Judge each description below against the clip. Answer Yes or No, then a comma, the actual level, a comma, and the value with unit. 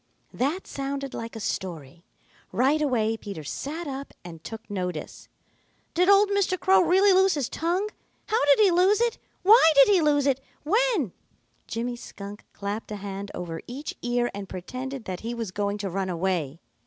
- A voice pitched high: Yes, high, 245 Hz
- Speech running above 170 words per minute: Yes, average, 180 wpm